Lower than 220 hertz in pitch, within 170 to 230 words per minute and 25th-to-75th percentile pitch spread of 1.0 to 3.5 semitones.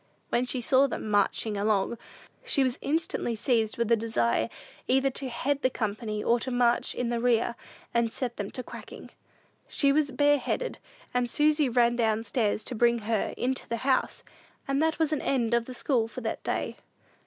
No: high, 240 Hz; average, 190 wpm; average, 2.9 semitones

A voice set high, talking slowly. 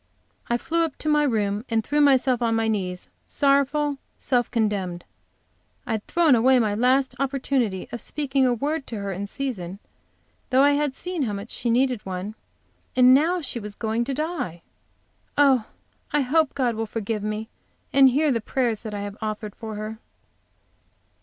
No: high, 245 Hz; average, 170 wpm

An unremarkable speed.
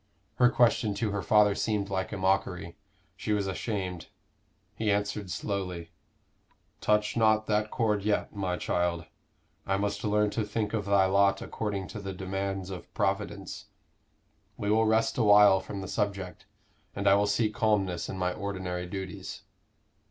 Yes: average, 160 wpm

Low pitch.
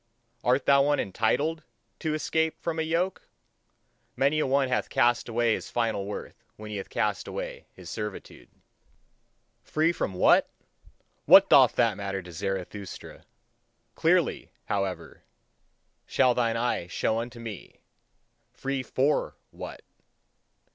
Yes: low, 120 Hz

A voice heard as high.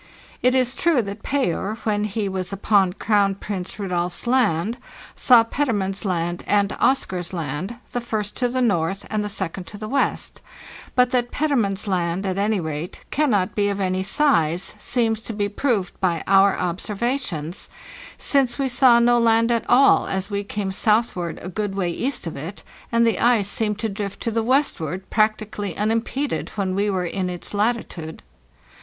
Yes: high, 205 Hz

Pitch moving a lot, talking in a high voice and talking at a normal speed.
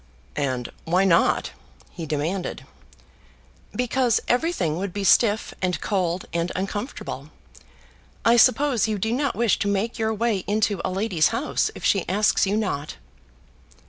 No: average, 4.2 semitones; high, 205 Hz; average, 145 wpm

